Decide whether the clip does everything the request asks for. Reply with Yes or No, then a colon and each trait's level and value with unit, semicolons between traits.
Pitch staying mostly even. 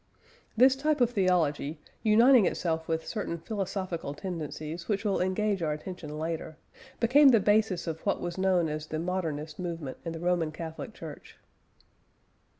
No: average, 4.4 semitones